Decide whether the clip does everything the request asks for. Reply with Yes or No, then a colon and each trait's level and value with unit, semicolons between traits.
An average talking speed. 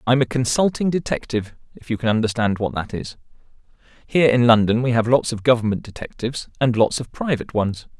Yes: average, 190 wpm